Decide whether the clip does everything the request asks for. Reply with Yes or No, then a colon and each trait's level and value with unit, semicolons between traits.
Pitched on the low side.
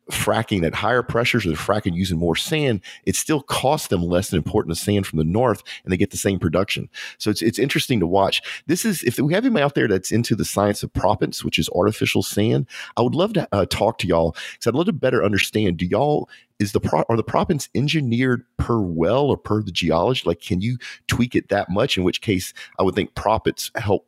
Yes: low, 105 Hz